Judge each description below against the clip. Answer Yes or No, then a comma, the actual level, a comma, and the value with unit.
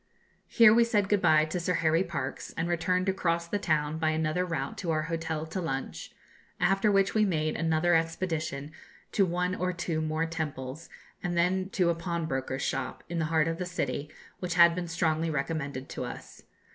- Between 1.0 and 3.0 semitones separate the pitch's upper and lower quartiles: Yes, narrow, 2.5 semitones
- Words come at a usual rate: Yes, average, 190 wpm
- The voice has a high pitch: No, medium, 165 Hz